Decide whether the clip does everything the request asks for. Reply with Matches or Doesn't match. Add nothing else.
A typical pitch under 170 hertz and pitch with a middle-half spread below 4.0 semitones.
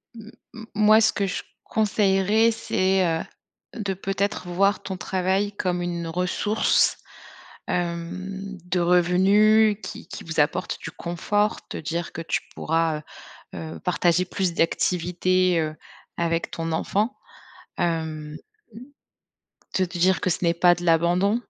Doesn't match